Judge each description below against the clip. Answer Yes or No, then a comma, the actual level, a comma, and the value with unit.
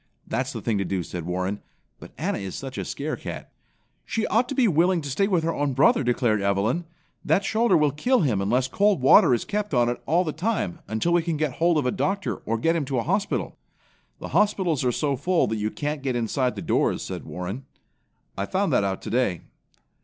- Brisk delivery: Yes, fast, 225 wpm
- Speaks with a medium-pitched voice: Yes, medium, 145 Hz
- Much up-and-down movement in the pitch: Yes, wide, 7.3 semitones